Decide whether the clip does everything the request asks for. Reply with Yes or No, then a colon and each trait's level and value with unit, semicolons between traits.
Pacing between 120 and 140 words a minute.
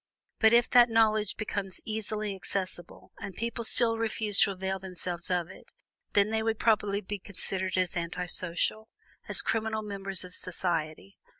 No: average, 160 wpm